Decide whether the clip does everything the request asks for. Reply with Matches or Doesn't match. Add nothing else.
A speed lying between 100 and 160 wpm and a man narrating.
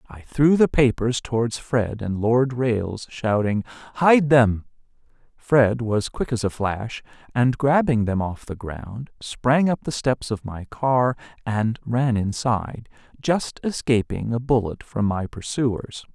Matches